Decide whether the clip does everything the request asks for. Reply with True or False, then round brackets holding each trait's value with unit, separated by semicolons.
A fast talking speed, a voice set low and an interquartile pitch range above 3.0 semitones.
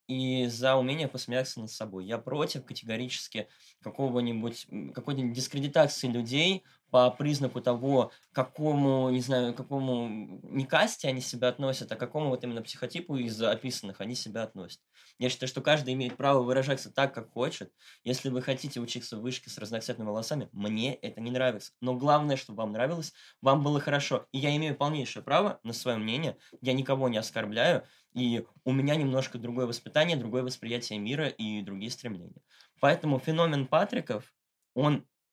False (165 wpm; 130 Hz; 2.5 semitones)